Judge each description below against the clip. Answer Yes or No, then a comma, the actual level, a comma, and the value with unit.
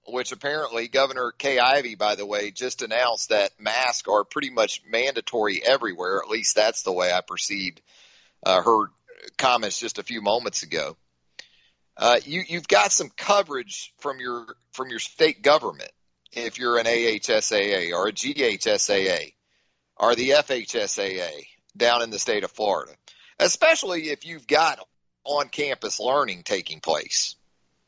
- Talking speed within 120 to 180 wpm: Yes, average, 150 wpm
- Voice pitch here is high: No, medium, 140 Hz